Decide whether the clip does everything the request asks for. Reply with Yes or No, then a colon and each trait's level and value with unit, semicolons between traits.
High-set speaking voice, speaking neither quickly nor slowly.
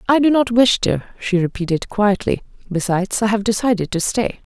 Yes: high, 210 Hz; average, 195 wpm